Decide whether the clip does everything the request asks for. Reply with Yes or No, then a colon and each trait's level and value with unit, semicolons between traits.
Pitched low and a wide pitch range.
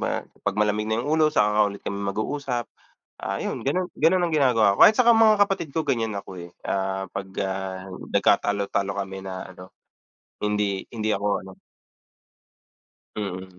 Yes: low, 105 Hz; wide, 6.1 semitones